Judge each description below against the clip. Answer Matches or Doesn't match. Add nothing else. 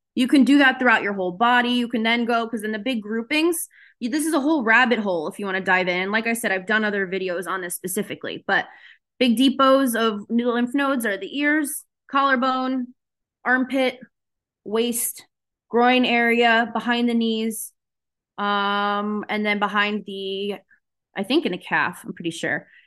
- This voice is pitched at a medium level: Doesn't match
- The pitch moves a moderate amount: Matches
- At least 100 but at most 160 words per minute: Doesn't match